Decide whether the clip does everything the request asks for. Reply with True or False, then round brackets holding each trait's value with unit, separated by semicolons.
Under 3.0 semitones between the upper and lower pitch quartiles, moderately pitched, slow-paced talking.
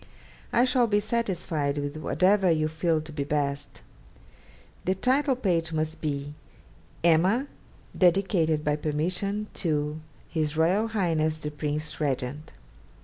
False (4.3 semitones; 160 Hz; 115 wpm)